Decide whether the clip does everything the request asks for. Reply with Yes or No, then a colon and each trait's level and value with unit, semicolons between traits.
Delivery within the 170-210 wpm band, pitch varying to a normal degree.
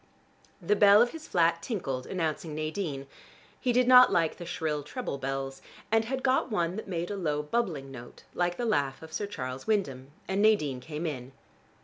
No: average, 190 wpm; wide, 6.9 semitones